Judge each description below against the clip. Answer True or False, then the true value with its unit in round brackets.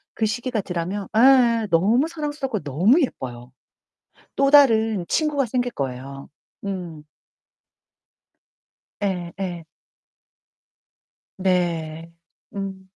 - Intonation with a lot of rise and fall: True (6.6 semitones)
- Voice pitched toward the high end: True (195 Hz)